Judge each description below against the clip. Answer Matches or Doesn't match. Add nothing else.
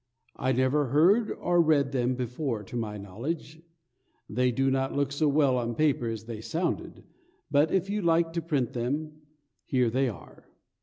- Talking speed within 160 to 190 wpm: Matches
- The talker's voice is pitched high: Doesn't match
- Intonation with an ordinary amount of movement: Matches